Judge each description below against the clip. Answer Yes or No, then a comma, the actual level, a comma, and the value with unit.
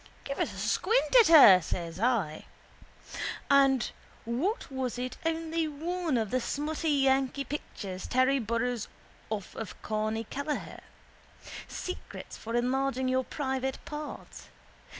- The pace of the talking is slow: Yes, slow, 125 wpm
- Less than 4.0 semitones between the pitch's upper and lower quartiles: No, average, 4.3 semitones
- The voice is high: Yes, very high, 265 Hz